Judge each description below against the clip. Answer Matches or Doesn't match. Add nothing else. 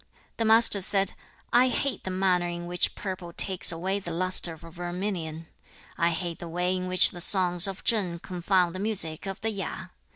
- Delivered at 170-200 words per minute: Matches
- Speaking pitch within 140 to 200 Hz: Matches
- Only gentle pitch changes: Matches